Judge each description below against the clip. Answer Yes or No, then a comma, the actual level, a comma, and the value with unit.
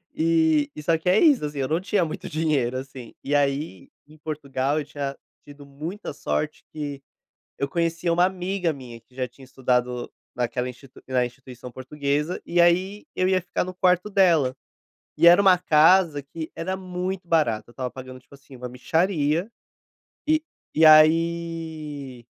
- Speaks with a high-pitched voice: No, medium, 150 Hz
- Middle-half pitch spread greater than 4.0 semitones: Yes, average, 4.4 semitones